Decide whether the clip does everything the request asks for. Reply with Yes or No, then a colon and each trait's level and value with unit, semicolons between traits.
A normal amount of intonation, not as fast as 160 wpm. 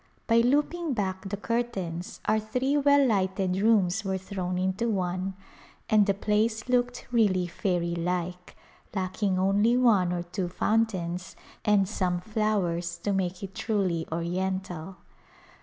Yes: average, 3.4 semitones; average, 140 wpm